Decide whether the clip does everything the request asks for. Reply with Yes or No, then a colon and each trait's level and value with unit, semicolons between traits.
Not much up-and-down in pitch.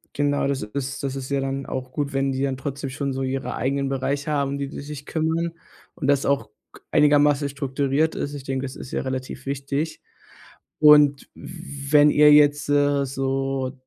Yes: narrow, 1.3 semitones